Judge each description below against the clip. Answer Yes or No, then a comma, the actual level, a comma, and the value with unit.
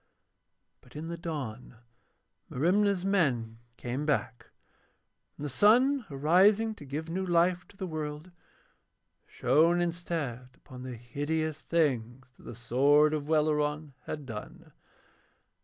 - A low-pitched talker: No, medium, 150 Hz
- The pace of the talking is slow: Yes, slow, 125 wpm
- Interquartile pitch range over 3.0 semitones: Yes, average, 4.8 semitones